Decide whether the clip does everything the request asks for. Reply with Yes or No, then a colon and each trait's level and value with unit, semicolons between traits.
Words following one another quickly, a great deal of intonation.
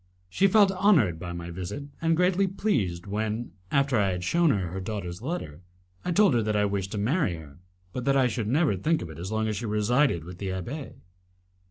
Yes: fast, 220 wpm; wide, 8.5 semitones